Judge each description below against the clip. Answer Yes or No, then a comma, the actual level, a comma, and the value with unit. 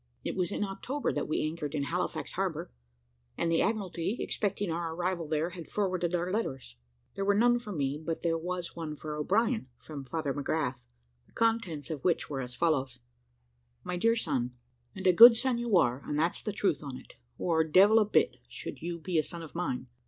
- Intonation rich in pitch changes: No, average, 4.8 semitones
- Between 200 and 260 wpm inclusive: Yes, fast, 205 wpm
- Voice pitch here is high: No, medium, 170 Hz